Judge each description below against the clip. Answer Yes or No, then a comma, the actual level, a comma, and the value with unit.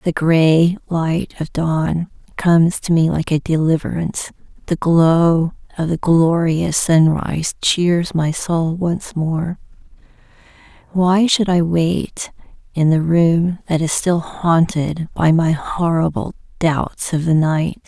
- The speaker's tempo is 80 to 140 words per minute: Yes, slow, 135 wpm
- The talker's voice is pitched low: No, medium, 165 Hz